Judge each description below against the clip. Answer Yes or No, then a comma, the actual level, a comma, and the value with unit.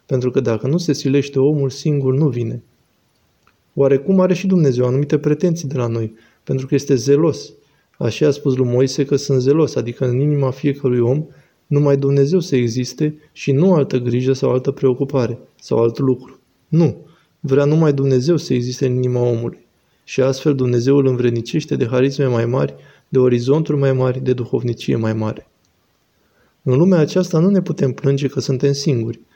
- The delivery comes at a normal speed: No, fast, 175 wpm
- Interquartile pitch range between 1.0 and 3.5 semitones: Yes, narrow, 2.5 semitones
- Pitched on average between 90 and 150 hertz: Yes, low, 135 Hz